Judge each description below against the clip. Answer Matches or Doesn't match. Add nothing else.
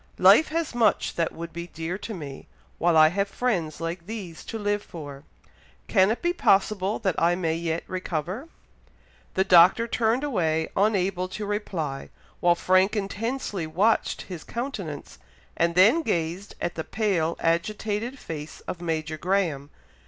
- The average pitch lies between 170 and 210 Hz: Matches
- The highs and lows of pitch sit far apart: Doesn't match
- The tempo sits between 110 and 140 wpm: Doesn't match